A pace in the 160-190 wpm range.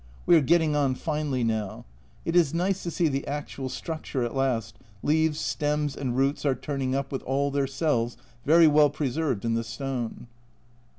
Yes: average, 180 wpm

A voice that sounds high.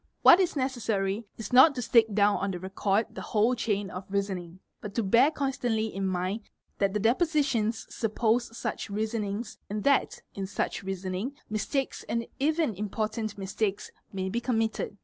Yes: high, 215 Hz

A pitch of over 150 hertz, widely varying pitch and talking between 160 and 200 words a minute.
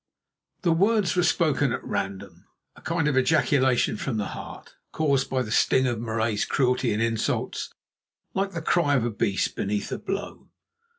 No: low, 130 Hz; wide, 6.6 semitones; average, 175 wpm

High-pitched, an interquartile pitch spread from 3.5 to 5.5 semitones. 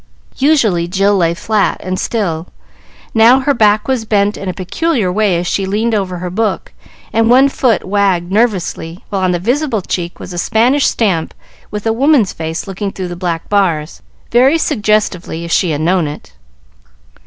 Yes: high, 200 Hz; average, 4.2 semitones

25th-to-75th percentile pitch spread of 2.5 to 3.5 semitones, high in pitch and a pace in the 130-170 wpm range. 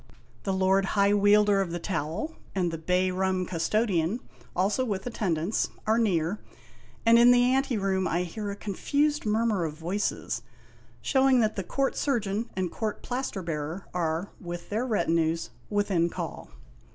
No: average, 4.2 semitones; high, 195 Hz; average, 155 wpm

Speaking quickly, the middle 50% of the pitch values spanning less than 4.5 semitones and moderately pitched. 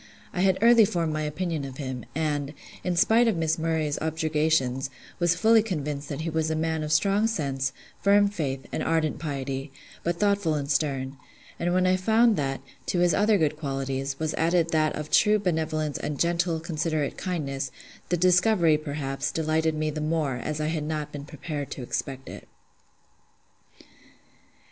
No: average, 170 wpm; average, 3.3 semitones; medium, 155 Hz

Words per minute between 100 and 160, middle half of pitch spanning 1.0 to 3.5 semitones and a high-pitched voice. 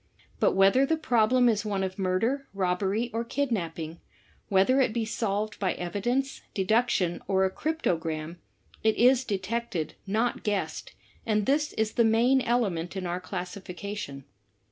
No: average, 145 wpm; average, 4.4 semitones; high, 210 Hz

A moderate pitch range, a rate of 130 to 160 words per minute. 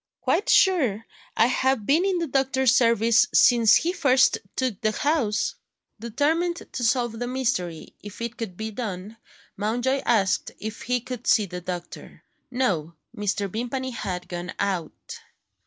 Yes: average, 4.3 semitones; average, 150 wpm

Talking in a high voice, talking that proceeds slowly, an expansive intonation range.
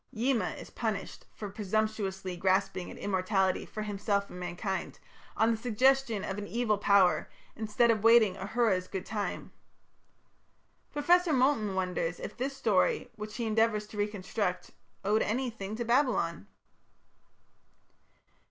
No: high, 210 Hz; slow, 130 wpm; average, 3.3 semitones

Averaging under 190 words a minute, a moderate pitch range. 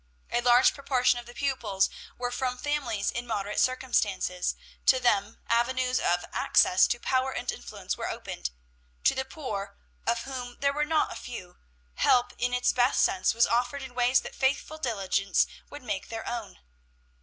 Yes: average, 170 wpm; average, 3.7 semitones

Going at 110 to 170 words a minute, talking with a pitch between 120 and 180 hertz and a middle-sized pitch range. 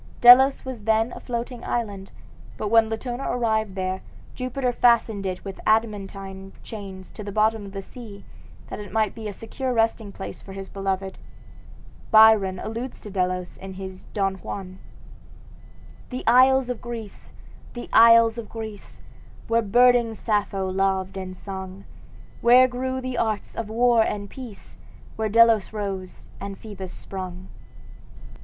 No: average, 150 wpm; high, 215 Hz; average, 3.2 semitones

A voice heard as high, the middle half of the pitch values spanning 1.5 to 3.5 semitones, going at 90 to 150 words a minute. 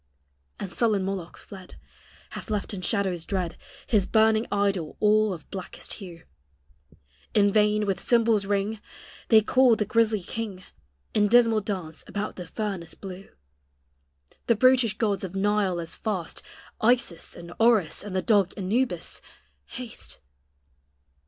Yes: high, 205 Hz; average, 2.8 semitones; slow, 135 wpm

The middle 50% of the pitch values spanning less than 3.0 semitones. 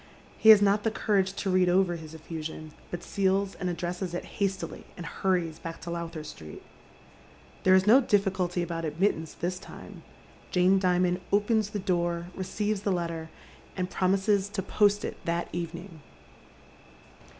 Yes: narrow, 2.6 semitones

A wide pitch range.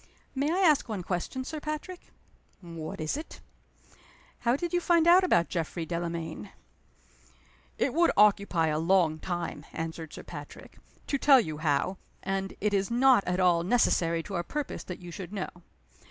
Yes: wide, 8.2 semitones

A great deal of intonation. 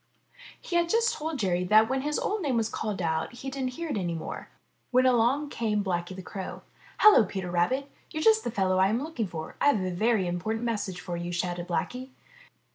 Yes: wide, 6.7 semitones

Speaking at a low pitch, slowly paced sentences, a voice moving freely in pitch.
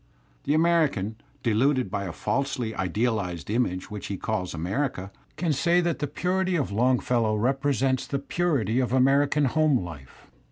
No: low, 125 Hz; average, 150 wpm; wide, 5.8 semitones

